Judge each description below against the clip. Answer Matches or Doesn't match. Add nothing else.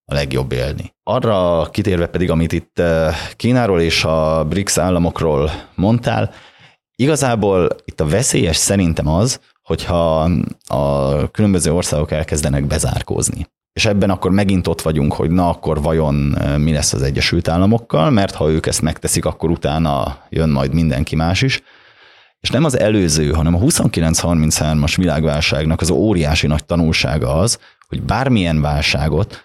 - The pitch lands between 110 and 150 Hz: Doesn't match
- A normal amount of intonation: Matches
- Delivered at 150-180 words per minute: Doesn't match